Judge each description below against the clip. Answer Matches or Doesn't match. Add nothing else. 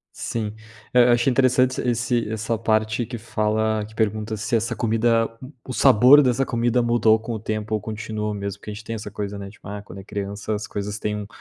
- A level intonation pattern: Matches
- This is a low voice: Matches